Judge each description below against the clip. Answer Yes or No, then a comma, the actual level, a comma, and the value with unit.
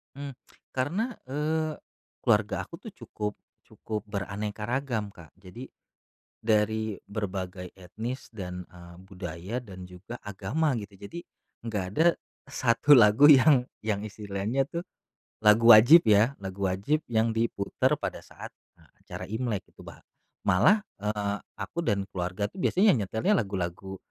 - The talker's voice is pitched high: No, low, 105 Hz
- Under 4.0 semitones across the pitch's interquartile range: No, average, 4.8 semitones